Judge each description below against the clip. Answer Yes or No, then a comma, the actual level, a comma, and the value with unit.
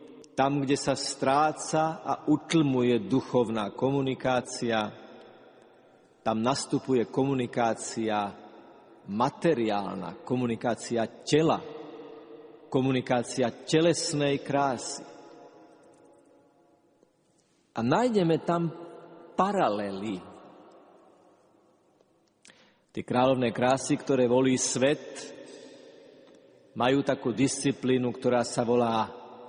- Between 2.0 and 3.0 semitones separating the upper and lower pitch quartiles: No, average, 3.8 semitones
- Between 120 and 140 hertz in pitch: Yes, low, 130 Hz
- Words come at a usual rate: No, slow, 65 wpm